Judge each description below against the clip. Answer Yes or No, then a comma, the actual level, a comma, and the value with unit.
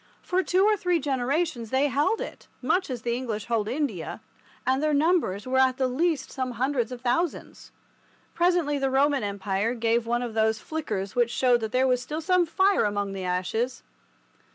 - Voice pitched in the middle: No, very high, 255 Hz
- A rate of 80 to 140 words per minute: No, average, 185 wpm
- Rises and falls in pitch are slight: No, average, 5.0 semitones